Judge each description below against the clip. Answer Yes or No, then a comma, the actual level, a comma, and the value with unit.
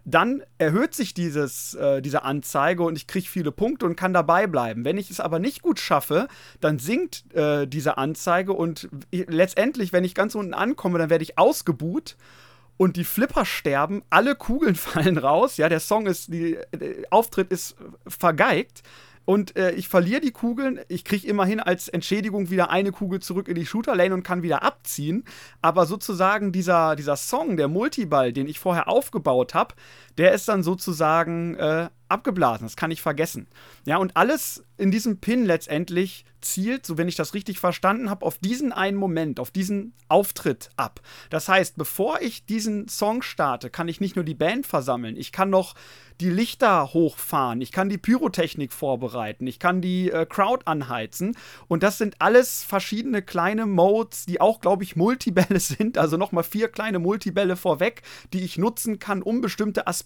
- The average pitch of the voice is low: No, medium, 185 Hz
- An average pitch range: Yes, average, 4.1 semitones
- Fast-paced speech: No, average, 180 wpm